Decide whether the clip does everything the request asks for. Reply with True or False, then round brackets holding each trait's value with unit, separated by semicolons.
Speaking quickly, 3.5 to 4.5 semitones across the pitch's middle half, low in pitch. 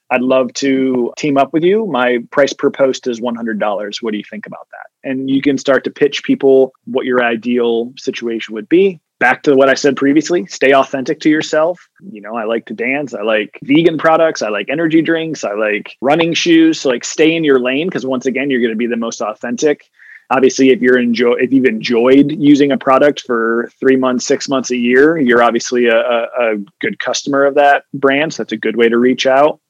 False (225 wpm; 3.0 semitones; 130 Hz)